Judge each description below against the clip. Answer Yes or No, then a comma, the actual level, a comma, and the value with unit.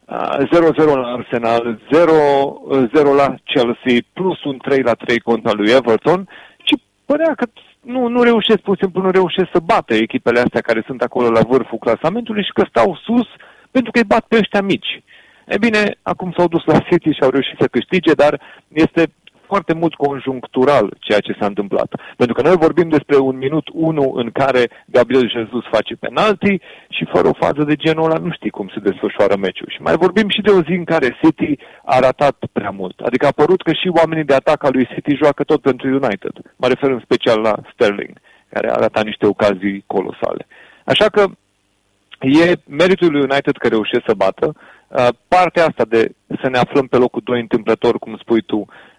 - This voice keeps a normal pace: No, fast, 190 wpm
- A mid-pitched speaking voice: Yes, medium, 145 Hz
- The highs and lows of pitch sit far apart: Yes, wide, 6.9 semitones